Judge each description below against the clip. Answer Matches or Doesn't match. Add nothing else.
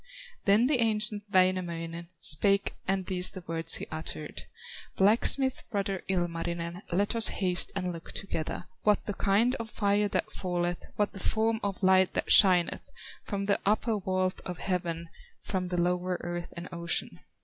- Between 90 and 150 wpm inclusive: Doesn't match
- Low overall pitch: Doesn't match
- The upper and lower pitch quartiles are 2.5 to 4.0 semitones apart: Matches